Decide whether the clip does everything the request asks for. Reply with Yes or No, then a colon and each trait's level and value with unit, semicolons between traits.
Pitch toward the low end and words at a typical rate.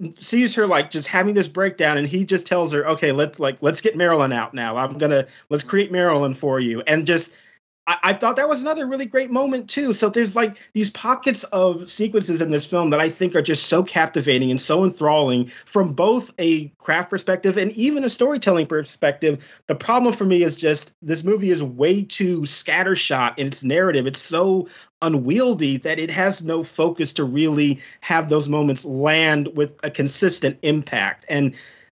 No: medium, 165 Hz; average, 190 wpm